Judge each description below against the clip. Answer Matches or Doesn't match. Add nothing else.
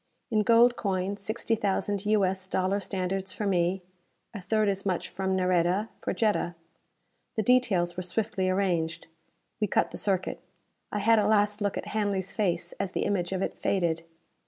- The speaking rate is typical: Matches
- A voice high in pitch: Matches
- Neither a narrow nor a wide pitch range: Doesn't match